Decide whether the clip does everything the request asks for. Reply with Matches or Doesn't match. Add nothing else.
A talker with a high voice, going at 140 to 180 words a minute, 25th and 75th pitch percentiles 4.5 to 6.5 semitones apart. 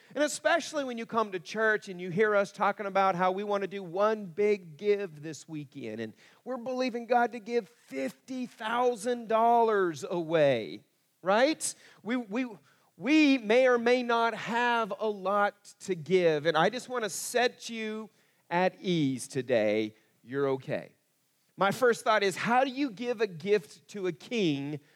Matches